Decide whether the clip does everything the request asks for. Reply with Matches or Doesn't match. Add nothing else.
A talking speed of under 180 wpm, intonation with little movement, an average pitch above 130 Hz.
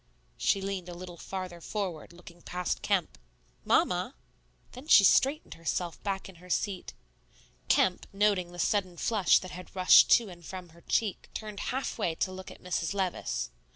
Matches